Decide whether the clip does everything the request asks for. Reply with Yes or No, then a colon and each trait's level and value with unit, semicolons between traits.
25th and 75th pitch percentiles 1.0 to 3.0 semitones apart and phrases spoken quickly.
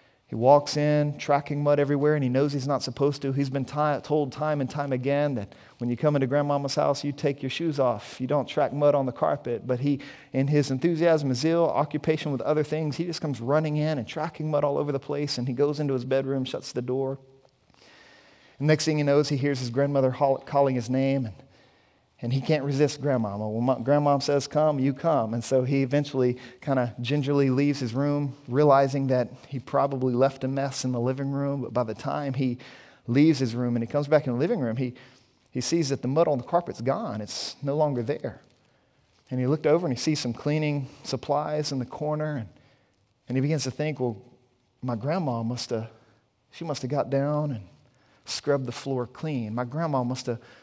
Yes: narrow, 2.6 semitones; fast, 220 wpm